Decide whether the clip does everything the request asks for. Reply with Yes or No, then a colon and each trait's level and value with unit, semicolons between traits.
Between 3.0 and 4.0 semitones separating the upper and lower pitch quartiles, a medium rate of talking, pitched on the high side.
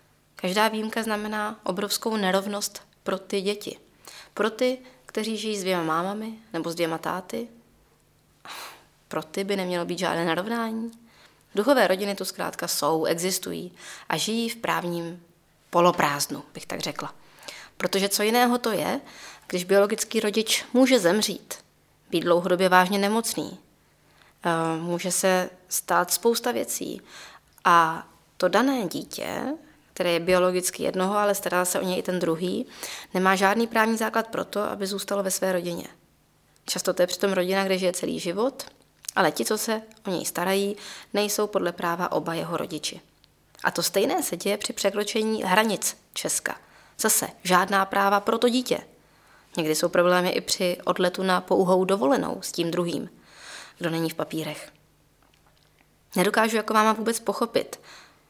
Yes: average, 3.4 semitones; average, 150 wpm; high, 195 Hz